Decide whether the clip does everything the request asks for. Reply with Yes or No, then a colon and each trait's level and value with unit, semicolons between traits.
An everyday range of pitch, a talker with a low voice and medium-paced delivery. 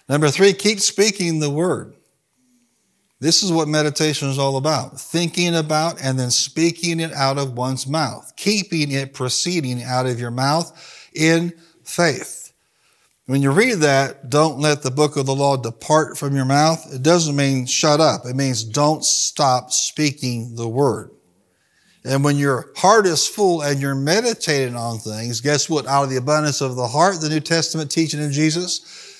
No: average, 3.4 semitones; medium, 150 Hz; average, 175 wpm